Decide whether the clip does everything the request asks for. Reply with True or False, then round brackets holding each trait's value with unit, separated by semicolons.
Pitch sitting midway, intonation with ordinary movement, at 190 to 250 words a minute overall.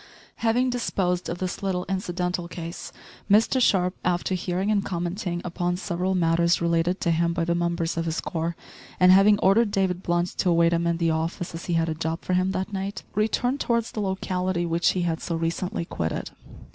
False (180 Hz; 2.1 semitones; 195 wpm)